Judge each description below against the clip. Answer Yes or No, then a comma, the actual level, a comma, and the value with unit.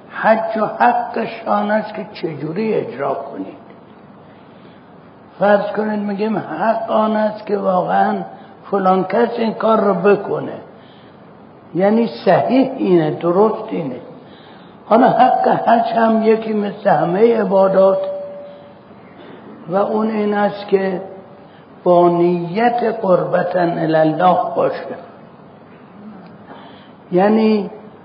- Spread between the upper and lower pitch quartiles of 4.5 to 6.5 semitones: No, narrow, 2.4 semitones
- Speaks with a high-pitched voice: Yes, high, 205 Hz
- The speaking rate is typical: No, slow, 100 wpm